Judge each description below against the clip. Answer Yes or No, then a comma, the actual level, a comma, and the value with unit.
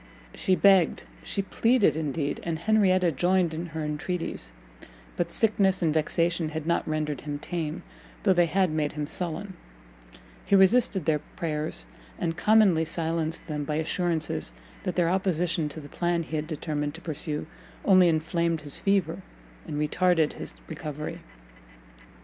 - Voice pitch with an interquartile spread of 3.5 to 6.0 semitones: No, average, 3.0 semitones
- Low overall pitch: No, medium, 165 Hz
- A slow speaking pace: No, average, 150 wpm